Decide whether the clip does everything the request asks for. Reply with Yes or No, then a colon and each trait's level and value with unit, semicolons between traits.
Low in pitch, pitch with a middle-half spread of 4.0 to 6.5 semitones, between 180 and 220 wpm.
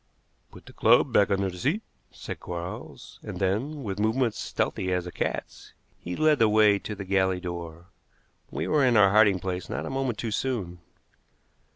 Yes: low, 100 Hz; average, 4.5 semitones; average, 185 wpm